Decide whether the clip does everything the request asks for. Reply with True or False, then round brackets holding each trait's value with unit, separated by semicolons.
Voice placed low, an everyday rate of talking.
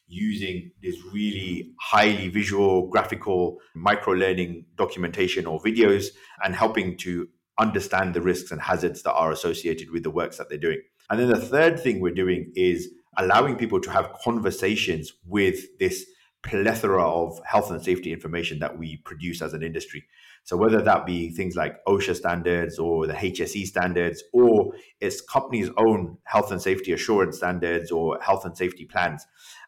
True (95 Hz; 165 wpm)